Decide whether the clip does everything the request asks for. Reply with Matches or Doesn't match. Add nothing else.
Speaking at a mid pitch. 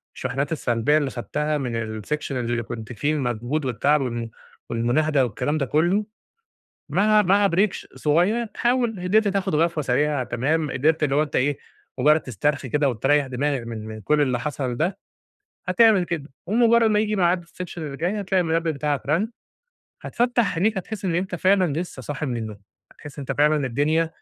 Matches